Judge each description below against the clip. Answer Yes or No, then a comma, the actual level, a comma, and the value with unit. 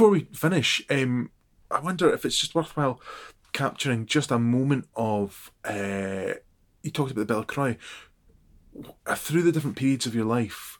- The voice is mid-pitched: No, low, 125 Hz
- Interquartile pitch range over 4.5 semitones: Yes, average, 5.2 semitones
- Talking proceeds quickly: No, average, 160 wpm